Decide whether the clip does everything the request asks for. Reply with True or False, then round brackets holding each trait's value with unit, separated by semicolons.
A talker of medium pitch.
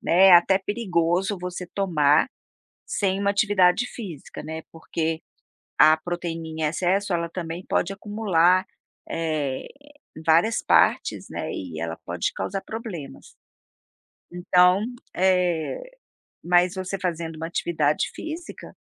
True (175 Hz)